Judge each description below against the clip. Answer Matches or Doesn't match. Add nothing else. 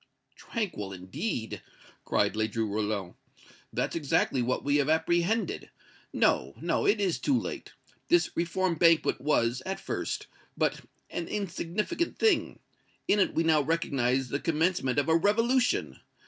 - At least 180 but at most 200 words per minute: Doesn't match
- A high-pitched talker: Doesn't match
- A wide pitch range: Matches